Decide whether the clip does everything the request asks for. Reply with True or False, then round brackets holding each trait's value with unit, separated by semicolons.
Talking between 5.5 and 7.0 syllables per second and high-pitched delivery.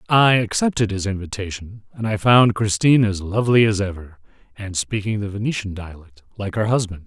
False (5.6 syllables/s; 105 Hz)